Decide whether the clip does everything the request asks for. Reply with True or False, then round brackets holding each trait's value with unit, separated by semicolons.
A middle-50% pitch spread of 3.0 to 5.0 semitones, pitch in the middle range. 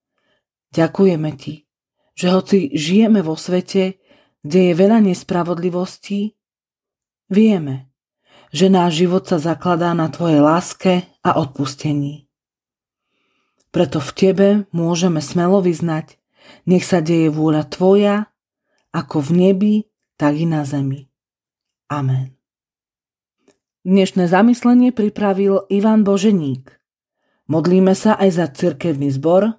True (4.1 semitones; 180 Hz)